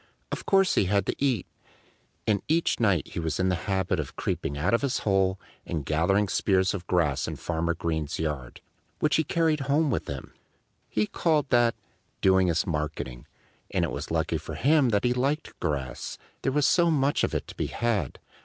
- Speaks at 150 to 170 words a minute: No, average, 195 wpm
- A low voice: Yes, very low, 95 Hz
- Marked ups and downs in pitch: Yes, wide, 8.5 semitones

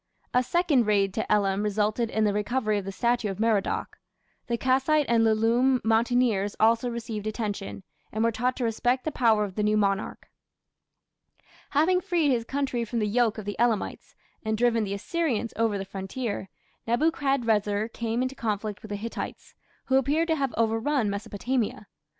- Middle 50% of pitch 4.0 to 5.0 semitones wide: No, average, 3.2 semitones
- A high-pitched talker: Yes, high, 225 Hz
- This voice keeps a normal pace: Yes, average, 170 wpm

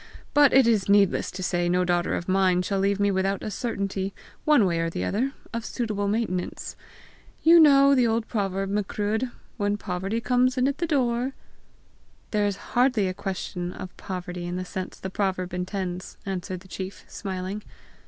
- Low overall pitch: No, high, 200 Hz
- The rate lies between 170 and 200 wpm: Yes, average, 185 wpm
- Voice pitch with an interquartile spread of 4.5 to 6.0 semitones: No, average, 4.0 semitones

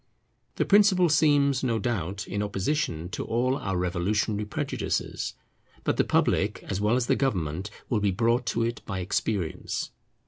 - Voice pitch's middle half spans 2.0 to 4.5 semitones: No, average, 4.9 semitones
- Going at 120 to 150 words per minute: No, average, 160 wpm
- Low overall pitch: Yes, low, 105 Hz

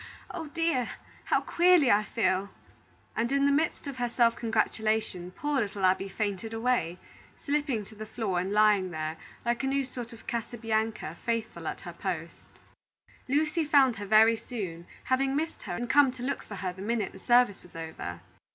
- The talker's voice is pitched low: No, high, 225 Hz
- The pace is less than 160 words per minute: No, average, 185 wpm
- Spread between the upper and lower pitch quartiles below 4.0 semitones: No, average, 5.2 semitones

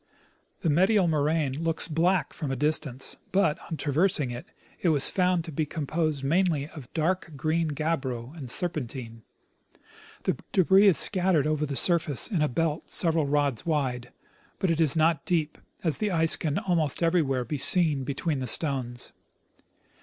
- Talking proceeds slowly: No, average, 165 wpm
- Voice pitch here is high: No, medium, 155 Hz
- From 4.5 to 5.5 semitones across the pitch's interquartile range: No, average, 3.3 semitones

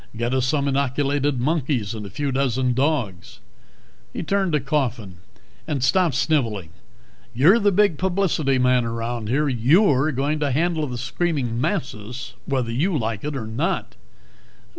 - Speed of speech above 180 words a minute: No, average, 150 wpm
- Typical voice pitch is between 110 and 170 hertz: Yes, low, 135 Hz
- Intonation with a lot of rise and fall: No, average, 4.2 semitones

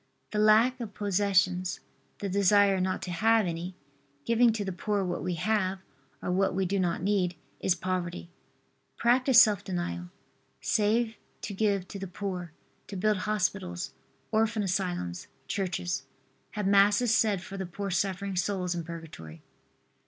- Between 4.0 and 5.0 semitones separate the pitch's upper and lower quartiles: No, average, 2.7 semitones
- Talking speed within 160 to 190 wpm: No, average, 150 wpm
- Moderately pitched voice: No, high, 195 Hz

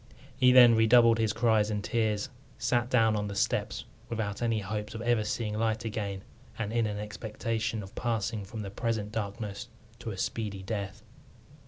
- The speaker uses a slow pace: No, average, 175 wpm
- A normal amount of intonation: No, narrow, 1.9 semitones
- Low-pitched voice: Yes, low, 110 Hz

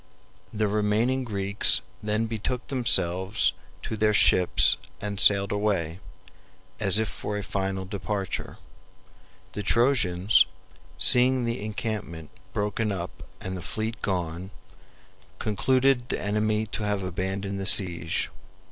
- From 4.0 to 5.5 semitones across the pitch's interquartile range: No, narrow, 2.4 semitones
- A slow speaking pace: Yes, slow, 120 wpm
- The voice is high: No, low, 105 Hz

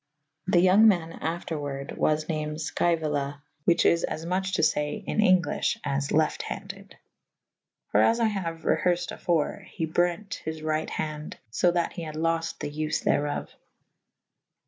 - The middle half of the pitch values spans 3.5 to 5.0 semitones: No, narrow, 2.5 semitones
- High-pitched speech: No, medium, 160 Hz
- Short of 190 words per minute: Yes, average, 170 wpm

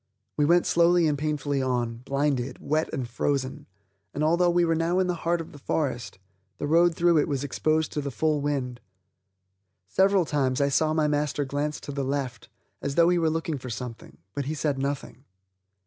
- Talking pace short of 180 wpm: No, average, 195 wpm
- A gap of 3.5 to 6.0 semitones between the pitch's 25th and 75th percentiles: No, average, 3.1 semitones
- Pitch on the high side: No, medium, 145 Hz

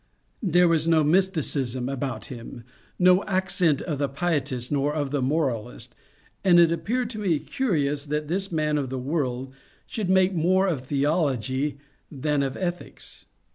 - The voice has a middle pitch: Yes, medium, 150 Hz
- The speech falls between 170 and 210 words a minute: No, average, 155 wpm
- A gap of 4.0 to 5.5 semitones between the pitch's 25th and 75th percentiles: Yes, average, 4.7 semitones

